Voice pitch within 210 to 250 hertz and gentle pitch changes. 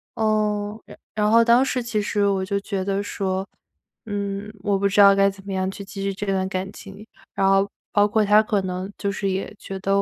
No: high, 200 Hz; narrow, 1.3 semitones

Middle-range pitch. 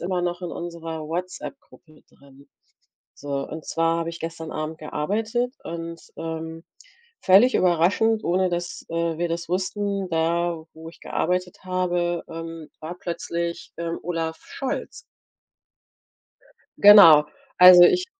Yes: medium, 170 Hz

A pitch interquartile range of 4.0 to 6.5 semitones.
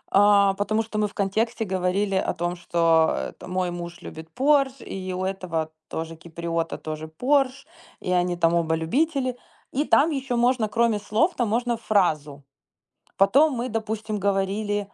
Yes: wide, 5.4 semitones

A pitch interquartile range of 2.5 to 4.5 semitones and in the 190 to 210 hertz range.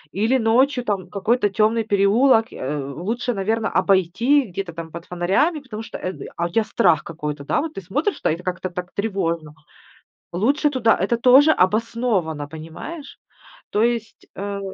No: wide, 5.4 semitones; high, 205 Hz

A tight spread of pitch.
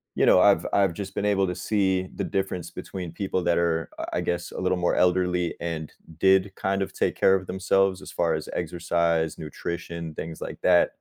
Yes: narrow, 2.1 semitones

